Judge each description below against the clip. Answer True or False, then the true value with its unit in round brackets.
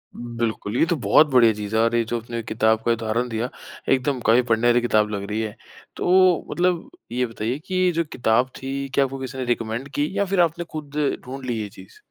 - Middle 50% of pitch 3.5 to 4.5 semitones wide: True (3.8 semitones)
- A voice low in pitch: True (120 Hz)